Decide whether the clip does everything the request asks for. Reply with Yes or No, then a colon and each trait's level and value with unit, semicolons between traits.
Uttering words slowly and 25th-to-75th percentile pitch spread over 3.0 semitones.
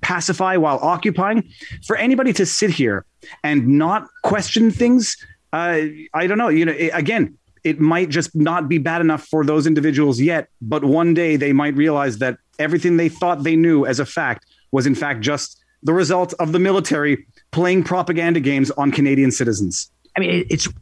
No: average, 185 wpm; average, 3.7 semitones